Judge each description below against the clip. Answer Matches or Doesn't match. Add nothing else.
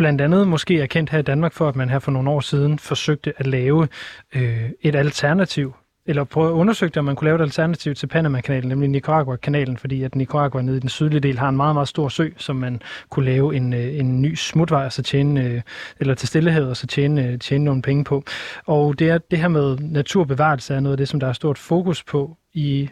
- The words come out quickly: Matches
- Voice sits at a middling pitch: Matches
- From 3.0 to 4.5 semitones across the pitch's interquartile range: Doesn't match